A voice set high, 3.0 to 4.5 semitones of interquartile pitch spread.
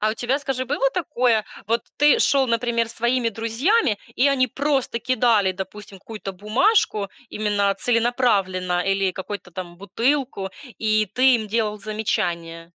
Yes: high, 225 Hz; average, 4.2 semitones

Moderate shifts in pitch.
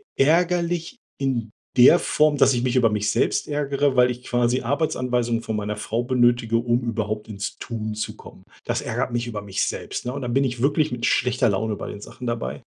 Yes: average, 3.5 semitones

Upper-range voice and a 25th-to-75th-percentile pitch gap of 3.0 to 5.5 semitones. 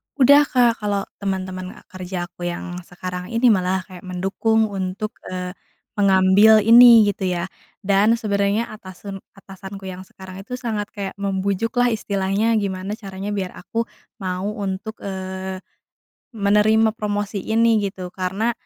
No: high, 200 Hz; narrow, 2.6 semitones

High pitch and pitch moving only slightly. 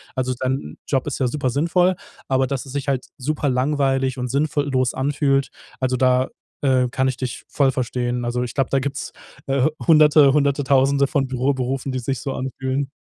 No: low, 135 Hz; narrow, 1.6 semitones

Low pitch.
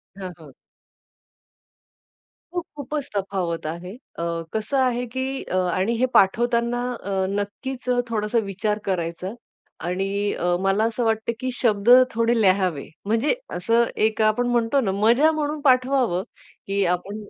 No: high, 220 Hz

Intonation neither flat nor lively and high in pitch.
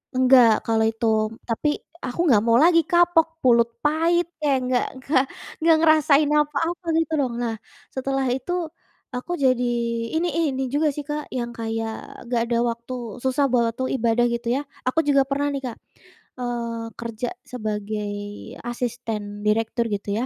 Yes: average, 4.3 semitones; very high, 250 Hz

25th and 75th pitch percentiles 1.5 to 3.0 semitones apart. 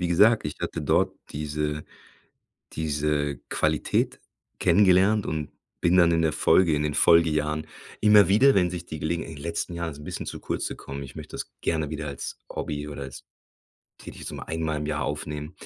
Yes: average, 2.7 semitones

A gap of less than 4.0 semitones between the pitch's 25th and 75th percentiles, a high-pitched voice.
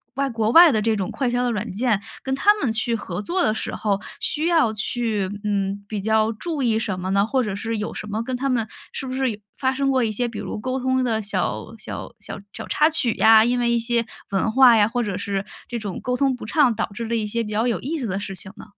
Yes: average, 3.5 semitones; high, 230 Hz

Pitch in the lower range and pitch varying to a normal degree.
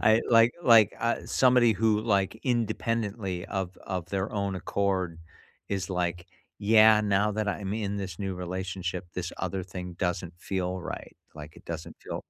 Yes: very low, 95 Hz; average, 3.1 semitones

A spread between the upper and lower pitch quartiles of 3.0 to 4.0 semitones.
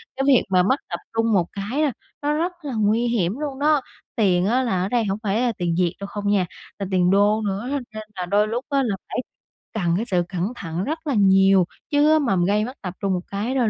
No: average, 4.8 semitones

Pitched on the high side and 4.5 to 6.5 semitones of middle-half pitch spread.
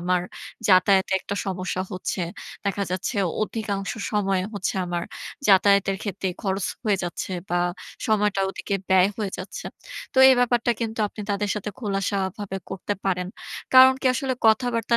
No: high, 200 Hz; narrow, 2.4 semitones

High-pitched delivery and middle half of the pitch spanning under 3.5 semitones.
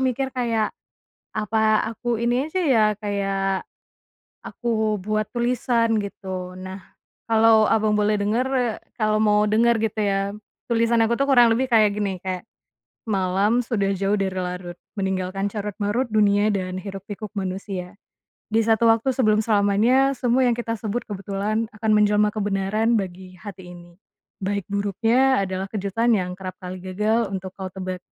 Yes: high, 210 Hz; average, 2.8 semitones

